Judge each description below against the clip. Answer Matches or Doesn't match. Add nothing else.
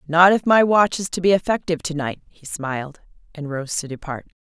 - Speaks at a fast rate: Matches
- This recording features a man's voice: Doesn't match